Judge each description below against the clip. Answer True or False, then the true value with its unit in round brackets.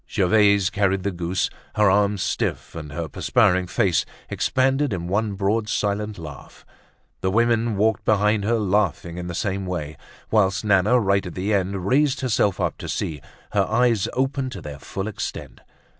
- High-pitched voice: False (100 Hz)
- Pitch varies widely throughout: False (2.9 semitones)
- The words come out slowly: False (170 wpm)